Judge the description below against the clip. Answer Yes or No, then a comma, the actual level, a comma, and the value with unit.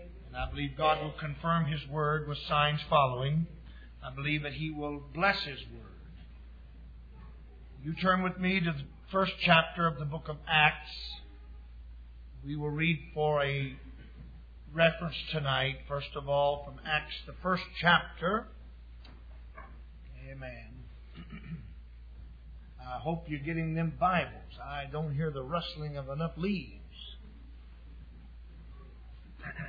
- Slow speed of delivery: Yes, slow, 125 wpm